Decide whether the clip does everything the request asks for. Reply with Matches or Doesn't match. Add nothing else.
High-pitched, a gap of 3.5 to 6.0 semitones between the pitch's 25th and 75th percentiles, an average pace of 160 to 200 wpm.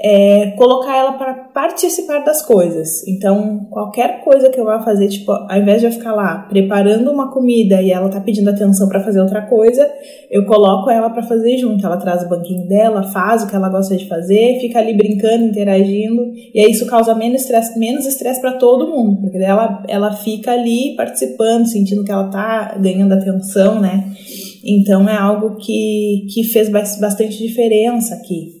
Doesn't match